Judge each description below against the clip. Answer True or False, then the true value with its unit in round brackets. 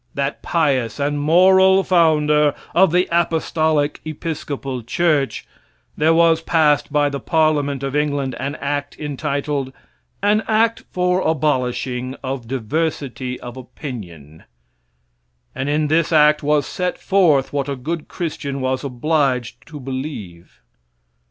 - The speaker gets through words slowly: True (125 wpm)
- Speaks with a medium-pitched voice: True (145 Hz)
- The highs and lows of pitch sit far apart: False (3.3 semitones)